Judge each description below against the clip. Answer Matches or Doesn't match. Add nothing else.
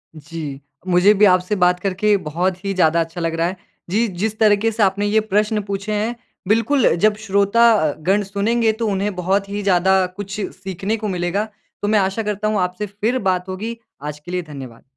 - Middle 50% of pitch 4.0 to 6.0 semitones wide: Doesn't match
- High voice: Matches